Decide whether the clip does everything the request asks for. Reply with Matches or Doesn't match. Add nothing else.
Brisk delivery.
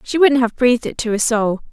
Matches